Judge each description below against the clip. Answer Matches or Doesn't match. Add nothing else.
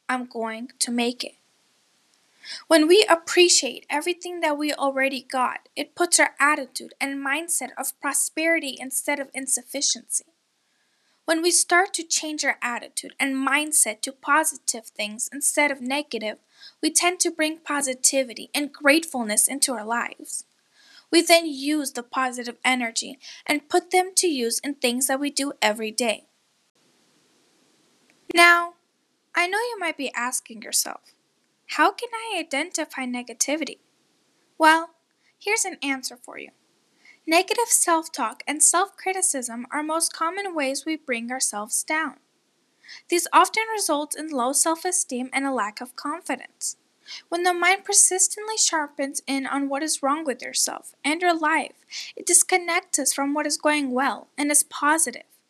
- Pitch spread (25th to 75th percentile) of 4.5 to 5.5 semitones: Doesn't match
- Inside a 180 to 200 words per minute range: Doesn't match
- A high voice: Matches